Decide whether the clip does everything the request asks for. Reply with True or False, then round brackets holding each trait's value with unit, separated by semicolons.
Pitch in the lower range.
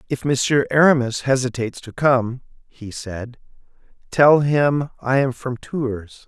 True (130 Hz)